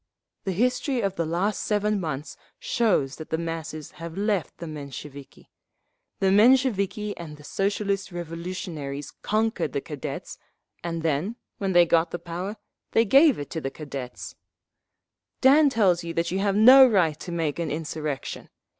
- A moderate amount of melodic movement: Yes, average, 4.8 semitones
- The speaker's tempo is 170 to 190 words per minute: No, average, 155 wpm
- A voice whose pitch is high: No, medium, 175 Hz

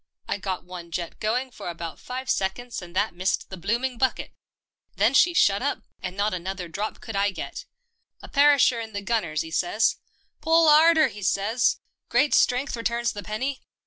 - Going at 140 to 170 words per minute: No, average, 190 wpm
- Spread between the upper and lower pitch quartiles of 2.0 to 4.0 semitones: No, wide, 5.5 semitones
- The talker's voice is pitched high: Yes, high, 215 Hz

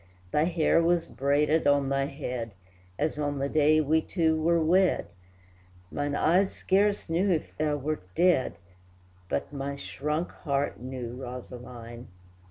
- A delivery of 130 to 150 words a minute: Yes, average, 140 wpm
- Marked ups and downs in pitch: No, average, 3.2 semitones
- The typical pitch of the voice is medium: Yes, medium, 150 Hz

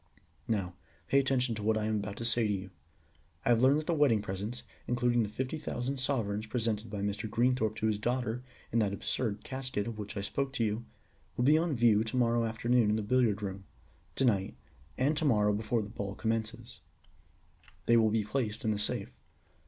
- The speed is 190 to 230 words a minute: Yes, fast, 205 wpm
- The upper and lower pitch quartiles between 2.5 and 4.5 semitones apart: Yes, average, 2.9 semitones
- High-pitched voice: No, low, 115 Hz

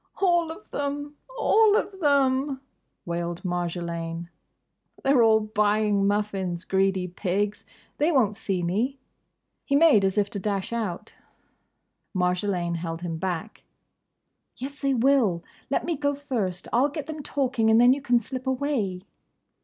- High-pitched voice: Yes, high, 220 Hz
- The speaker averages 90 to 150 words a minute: Yes, average, 140 wpm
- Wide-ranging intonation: Yes, wide, 7.2 semitones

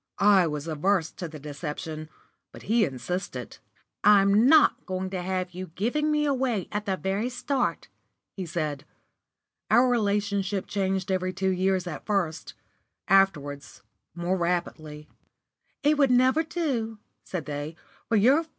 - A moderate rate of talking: No, slow, 115 wpm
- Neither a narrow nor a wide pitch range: Yes, average, 3.4 semitones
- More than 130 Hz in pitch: Yes, high, 190 Hz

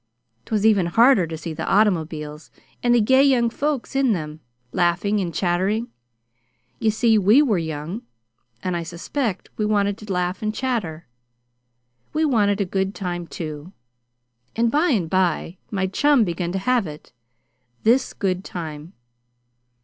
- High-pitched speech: Yes, high, 195 Hz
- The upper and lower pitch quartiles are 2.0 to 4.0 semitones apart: No, average, 4.9 semitones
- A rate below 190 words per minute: Yes, average, 150 wpm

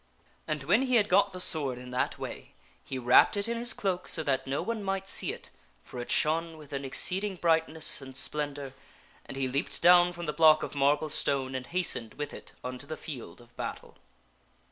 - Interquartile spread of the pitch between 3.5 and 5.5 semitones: Yes, average, 5.1 semitones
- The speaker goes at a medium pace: No, fast, 210 wpm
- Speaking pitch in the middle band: Yes, medium, 155 Hz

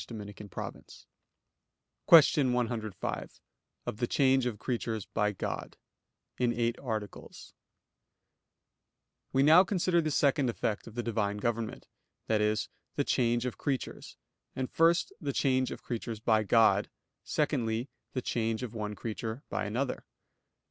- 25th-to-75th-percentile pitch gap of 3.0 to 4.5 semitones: Yes, average, 3.3 semitones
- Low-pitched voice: Yes, low, 120 Hz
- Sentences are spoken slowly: Yes, slow, 130 wpm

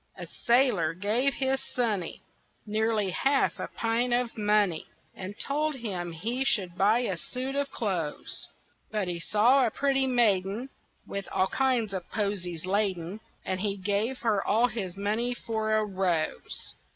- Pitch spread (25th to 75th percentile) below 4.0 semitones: No, average, 4.3 semitones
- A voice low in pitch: No, high, 215 Hz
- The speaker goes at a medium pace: Yes, average, 150 wpm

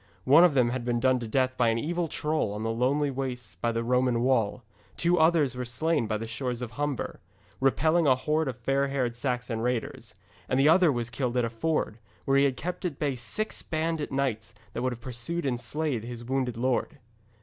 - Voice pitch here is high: No, low, 130 Hz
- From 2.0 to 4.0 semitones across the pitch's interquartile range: Yes, average, 3.7 semitones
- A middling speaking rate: No, fast, 215 wpm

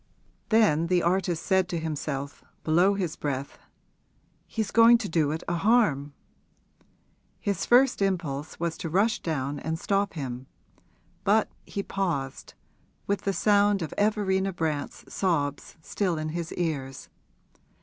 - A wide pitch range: No, average, 4.7 semitones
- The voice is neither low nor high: Yes, medium, 175 Hz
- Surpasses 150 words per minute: No, slow, 135 wpm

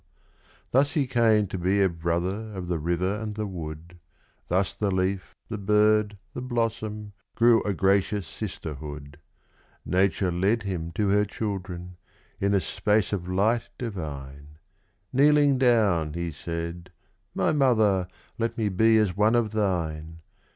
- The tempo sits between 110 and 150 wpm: Yes, average, 145 wpm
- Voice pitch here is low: Yes, low, 100 Hz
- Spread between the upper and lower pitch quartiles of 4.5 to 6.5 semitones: No, average, 3.9 semitones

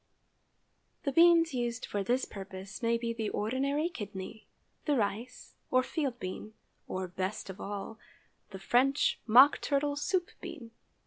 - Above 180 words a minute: No, average, 150 wpm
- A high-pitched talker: Yes, high, 235 Hz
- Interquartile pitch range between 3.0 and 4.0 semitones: No, wide, 5.4 semitones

